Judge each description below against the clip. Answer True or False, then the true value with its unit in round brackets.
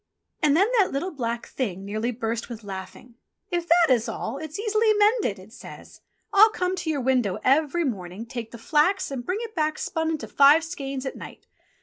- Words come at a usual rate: False (210 wpm)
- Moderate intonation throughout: False (6.9 semitones)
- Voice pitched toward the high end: True (280 Hz)